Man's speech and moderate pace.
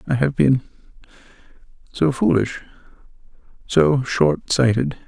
No: male; slow, 70 wpm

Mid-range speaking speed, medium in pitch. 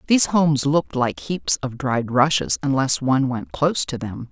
No: average, 195 wpm; low, 130 Hz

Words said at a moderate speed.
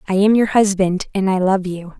No: fast, 240 wpm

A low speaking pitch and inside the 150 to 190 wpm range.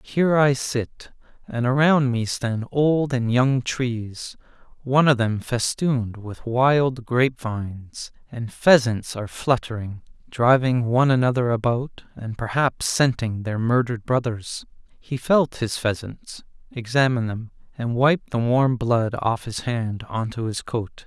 No: low, 120 Hz; average, 140 wpm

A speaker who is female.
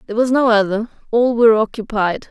Yes: female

